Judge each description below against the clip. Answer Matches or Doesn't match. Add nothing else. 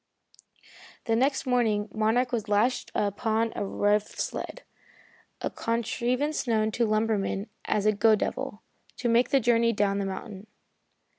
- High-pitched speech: Matches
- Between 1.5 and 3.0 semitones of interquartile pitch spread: Matches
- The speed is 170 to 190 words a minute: Doesn't match